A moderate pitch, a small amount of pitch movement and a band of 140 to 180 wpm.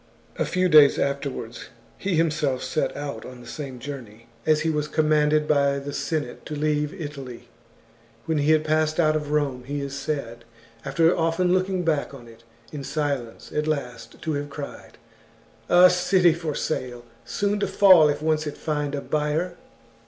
Yes: medium, 150 Hz; narrow, 2.3 semitones; average, 175 wpm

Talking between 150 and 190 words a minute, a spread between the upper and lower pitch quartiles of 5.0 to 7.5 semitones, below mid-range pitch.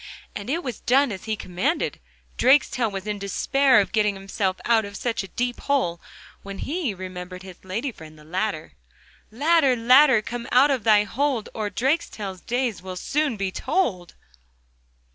No: average, 165 wpm; wide, 5.4 semitones; high, 220 Hz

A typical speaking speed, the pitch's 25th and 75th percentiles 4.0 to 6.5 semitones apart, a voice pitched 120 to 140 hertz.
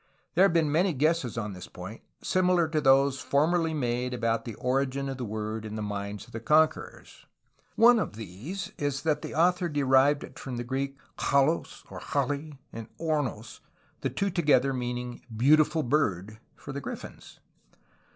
Yes: average, 170 wpm; average, 5.0 semitones; low, 135 Hz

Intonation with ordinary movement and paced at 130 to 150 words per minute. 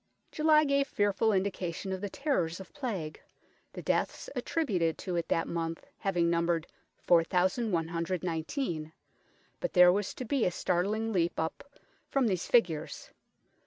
Yes: average, 5.0 semitones; slow, 135 wpm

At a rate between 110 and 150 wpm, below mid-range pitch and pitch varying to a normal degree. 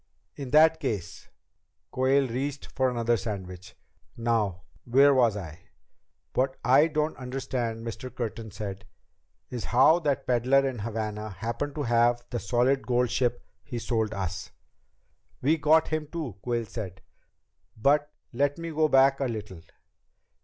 Yes: average, 145 wpm; low, 120 Hz; average, 3.8 semitones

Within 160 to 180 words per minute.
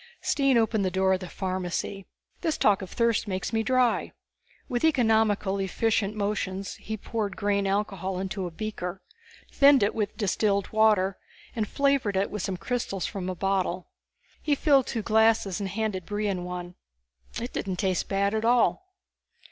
Yes: average, 165 wpm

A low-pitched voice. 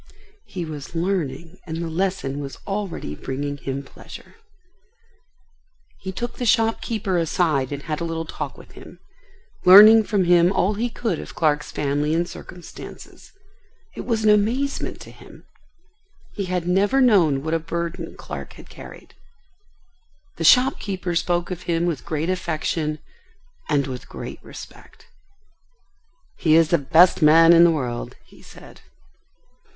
No: medium, 170 Hz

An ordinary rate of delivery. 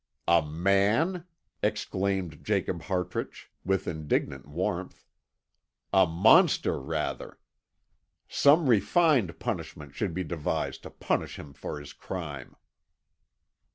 No: slow, 100 wpm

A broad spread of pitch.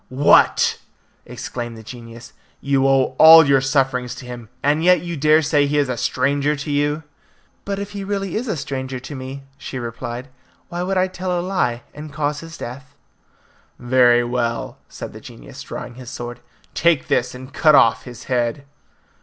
No: average, 4.1 semitones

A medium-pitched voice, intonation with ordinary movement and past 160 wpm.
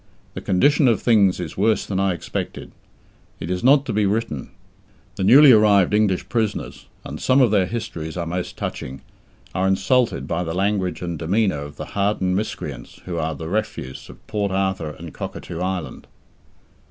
No: very low, 95 Hz; average, 4.2 semitones; average, 175 wpm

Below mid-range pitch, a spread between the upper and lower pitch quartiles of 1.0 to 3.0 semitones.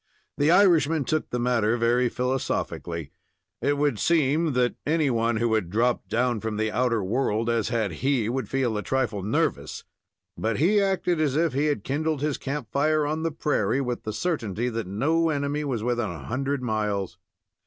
No: low, 125 Hz; average, 4.9 semitones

